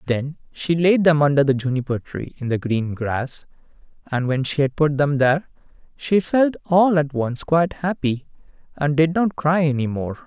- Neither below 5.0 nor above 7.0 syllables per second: No, 4.7 syllables/s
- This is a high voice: No, medium, 150 Hz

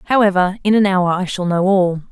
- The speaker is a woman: Yes, female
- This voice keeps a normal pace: No, fast, 225 wpm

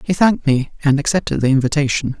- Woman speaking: No, male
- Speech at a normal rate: Yes, average, 190 wpm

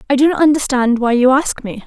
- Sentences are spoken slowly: No, fast, 255 wpm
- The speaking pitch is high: Yes, very high, 265 Hz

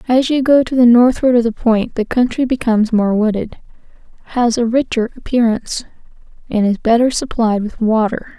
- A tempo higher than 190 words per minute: No, average, 170 wpm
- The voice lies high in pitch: Yes, high, 235 Hz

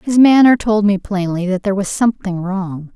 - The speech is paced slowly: No, fast, 205 wpm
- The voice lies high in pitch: Yes, high, 200 Hz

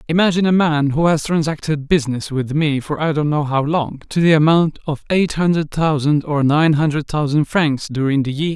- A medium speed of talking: No, fast, 210 wpm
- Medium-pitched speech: Yes, medium, 150 Hz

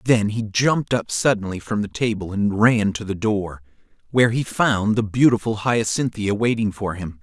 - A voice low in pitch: Yes, low, 110 Hz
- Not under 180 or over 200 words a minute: Yes, average, 185 wpm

